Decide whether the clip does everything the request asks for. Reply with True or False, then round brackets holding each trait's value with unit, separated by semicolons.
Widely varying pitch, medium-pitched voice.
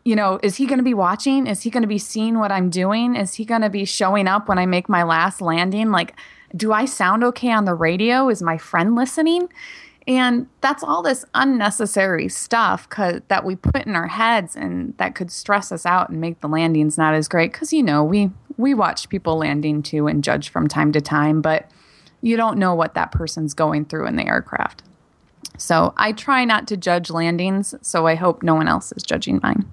False (5.7 semitones; 195 Hz)